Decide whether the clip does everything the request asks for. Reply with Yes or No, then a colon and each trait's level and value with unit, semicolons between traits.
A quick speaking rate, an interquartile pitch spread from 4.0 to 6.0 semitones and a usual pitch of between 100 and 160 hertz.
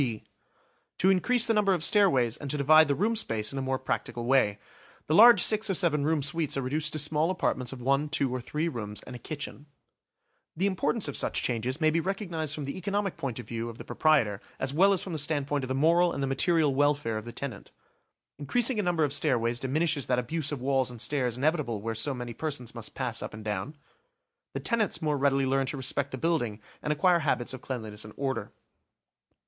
Yes: fast, 225 wpm; average, 4.6 semitones; medium, 140 Hz